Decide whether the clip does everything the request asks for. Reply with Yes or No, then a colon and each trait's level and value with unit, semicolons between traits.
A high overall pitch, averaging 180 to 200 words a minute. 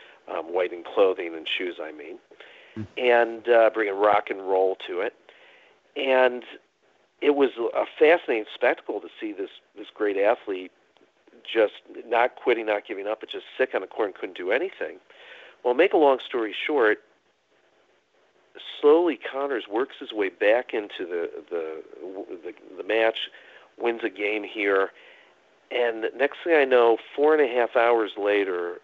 No: very high, 375 Hz; average, 165 wpm